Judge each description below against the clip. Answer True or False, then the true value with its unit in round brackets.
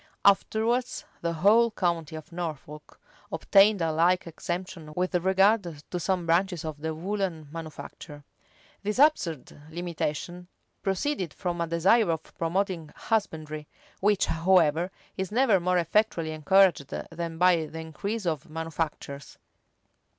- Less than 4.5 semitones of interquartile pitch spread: True (3.3 semitones)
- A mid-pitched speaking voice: True (175 Hz)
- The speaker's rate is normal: False (130 wpm)